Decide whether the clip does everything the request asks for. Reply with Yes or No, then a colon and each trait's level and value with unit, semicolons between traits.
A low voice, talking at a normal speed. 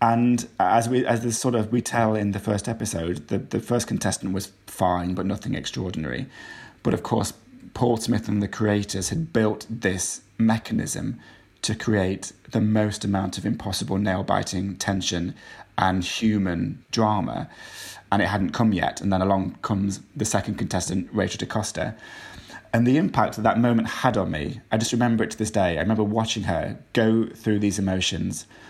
Yes: low, 105 Hz; average, 175 wpm